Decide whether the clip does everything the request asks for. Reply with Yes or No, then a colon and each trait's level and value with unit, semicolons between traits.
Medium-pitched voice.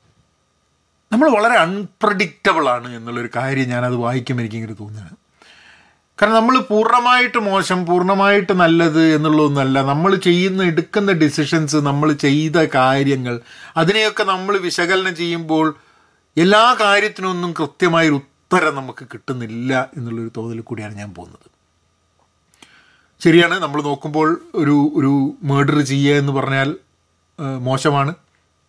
Yes: medium, 150 Hz